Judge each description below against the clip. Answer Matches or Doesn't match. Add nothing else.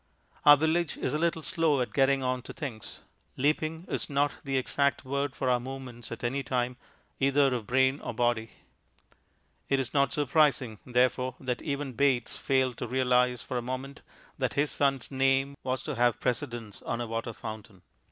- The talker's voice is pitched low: Matches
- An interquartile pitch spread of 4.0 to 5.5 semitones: Doesn't match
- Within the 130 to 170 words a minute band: Doesn't match